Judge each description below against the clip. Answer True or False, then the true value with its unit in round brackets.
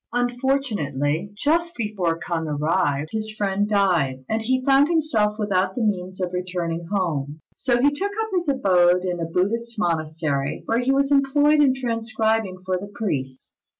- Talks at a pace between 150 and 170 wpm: True (160 wpm)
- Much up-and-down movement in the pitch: True (6.3 semitones)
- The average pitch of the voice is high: True (205 Hz)